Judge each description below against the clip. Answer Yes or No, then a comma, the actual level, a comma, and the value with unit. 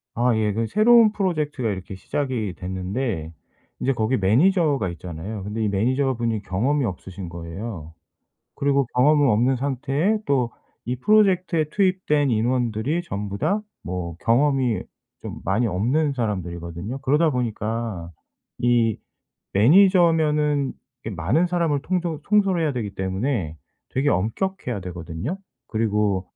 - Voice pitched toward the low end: Yes, low, 120 Hz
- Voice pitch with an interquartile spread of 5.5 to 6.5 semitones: No, wide, 7.1 semitones